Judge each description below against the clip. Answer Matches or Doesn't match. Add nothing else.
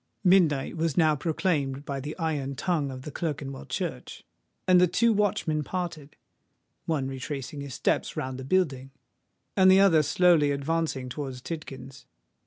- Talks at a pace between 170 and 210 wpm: Doesn't match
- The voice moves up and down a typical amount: Matches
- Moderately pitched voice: Matches